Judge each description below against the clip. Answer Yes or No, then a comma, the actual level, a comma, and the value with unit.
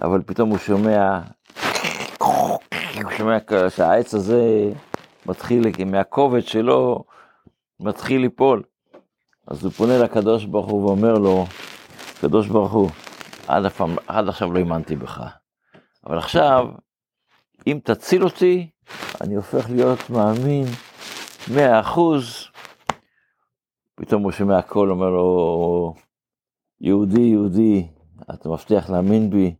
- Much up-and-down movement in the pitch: No, average, 3.7 semitones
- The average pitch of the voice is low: Yes, low, 105 Hz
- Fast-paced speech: No, average, 110 wpm